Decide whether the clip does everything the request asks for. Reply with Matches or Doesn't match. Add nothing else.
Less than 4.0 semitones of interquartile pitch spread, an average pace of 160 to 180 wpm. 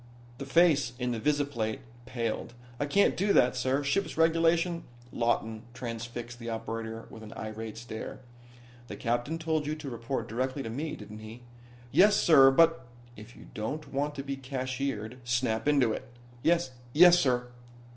Doesn't match